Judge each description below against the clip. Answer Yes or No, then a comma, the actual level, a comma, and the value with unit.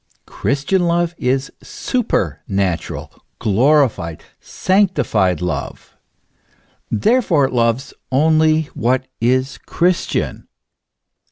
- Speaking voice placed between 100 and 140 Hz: Yes, low, 135 Hz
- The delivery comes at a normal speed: No, slow, 75 wpm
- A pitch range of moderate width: No, wide, 6.9 semitones